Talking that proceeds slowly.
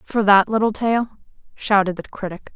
No: average, 165 wpm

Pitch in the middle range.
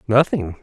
No: low, 120 Hz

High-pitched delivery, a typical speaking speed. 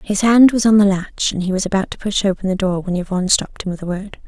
No: high, 195 Hz; fast, 310 wpm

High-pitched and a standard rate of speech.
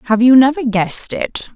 Yes: high, 245 Hz; average, 195 wpm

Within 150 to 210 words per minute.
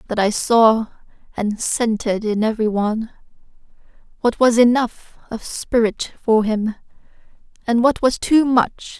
No: slow, 135 wpm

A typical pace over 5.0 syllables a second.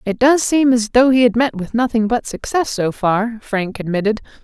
No: 4.9 syllables/s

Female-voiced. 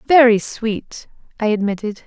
Yes: female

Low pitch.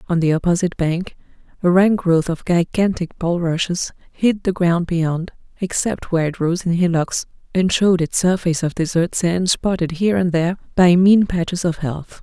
No: medium, 175 Hz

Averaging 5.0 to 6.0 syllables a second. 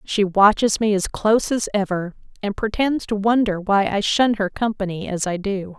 No: 4.8 syllables/s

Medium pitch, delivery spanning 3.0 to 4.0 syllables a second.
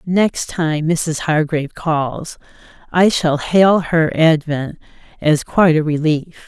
Yes: medium, 160 Hz; 3.6 syllables/s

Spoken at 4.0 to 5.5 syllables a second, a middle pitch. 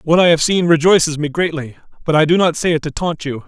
No: 6.2 syllables/s; medium, 160 Hz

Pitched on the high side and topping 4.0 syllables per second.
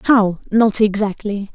No: high, 205 Hz; 3.9 syllables/s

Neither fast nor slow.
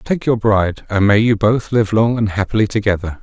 No: fast, 225 wpm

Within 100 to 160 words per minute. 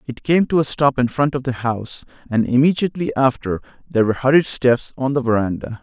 No: fast, 205 wpm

